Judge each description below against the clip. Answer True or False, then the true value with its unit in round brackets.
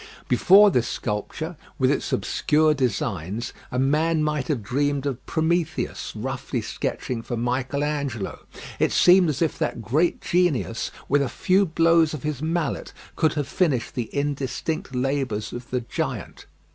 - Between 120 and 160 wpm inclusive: True (150 wpm)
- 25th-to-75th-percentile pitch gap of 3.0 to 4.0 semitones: False (4.4 semitones)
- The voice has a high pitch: False (140 Hz)